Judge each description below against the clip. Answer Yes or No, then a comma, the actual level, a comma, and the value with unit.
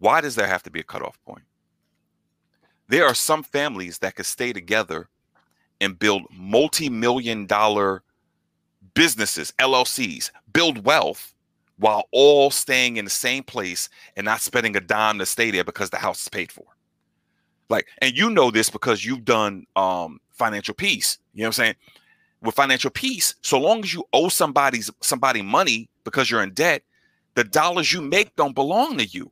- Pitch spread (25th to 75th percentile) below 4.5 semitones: No, average, 5.2 semitones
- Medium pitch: No, low, 115 Hz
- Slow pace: No, average, 175 wpm